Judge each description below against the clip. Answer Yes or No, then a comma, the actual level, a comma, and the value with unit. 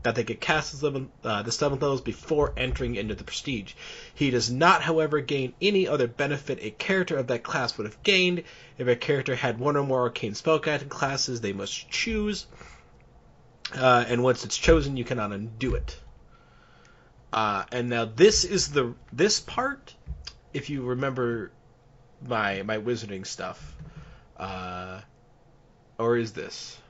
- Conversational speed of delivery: Yes, average, 155 wpm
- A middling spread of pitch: Yes, average, 4.2 semitones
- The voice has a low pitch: Yes, low, 125 Hz